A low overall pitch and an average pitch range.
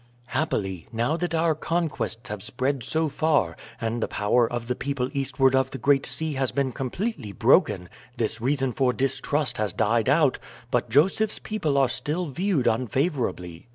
Yes: low, 130 Hz; average, 4.5 semitones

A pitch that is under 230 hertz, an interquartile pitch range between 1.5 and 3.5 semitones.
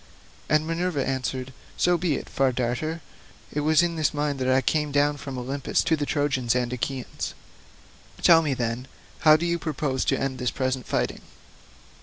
Yes: medium, 140 Hz; average, 3.2 semitones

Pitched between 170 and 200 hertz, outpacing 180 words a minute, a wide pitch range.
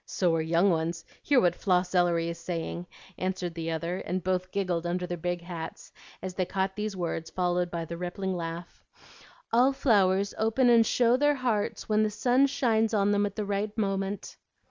No: medium, 185 Hz; average, 190 wpm; average, 3.5 semitones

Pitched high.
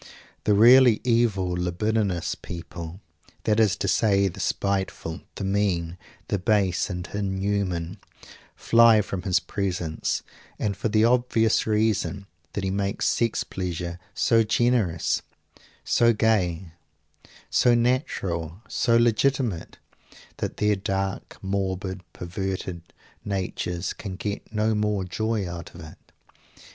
No: low, 100 Hz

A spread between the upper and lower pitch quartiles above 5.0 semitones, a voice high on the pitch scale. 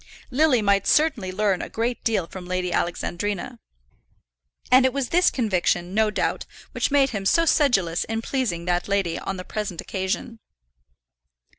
Yes: wide, 5.4 semitones; high, 205 Hz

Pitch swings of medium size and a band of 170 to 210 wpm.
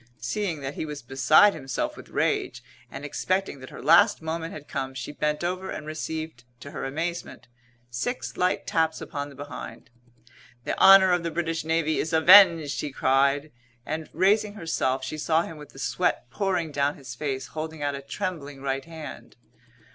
Yes: average, 3.3 semitones; average, 175 wpm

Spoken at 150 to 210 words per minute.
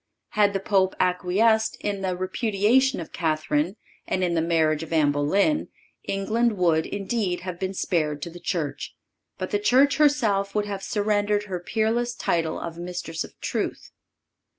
Yes: average, 160 wpm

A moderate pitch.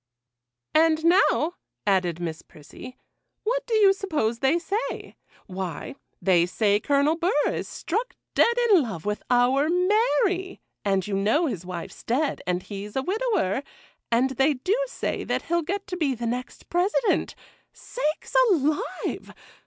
No: very high, 290 Hz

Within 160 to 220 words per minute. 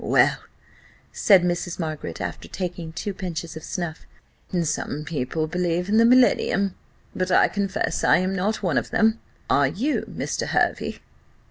No: average, 150 wpm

